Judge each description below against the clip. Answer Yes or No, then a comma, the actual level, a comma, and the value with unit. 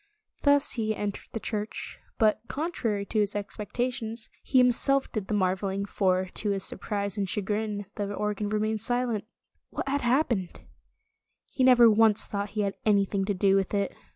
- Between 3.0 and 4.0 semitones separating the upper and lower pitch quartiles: No, narrow, 2.6 semitones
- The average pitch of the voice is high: Yes, high, 210 Hz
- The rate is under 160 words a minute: No, average, 175 wpm